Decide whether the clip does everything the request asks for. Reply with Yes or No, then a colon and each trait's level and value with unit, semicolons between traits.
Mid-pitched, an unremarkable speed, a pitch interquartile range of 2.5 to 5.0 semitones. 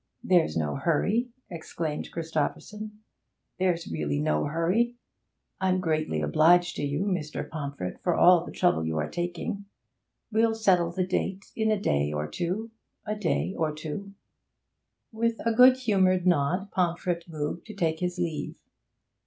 Yes: medium, 175 Hz; average, 145 wpm; average, 4.5 semitones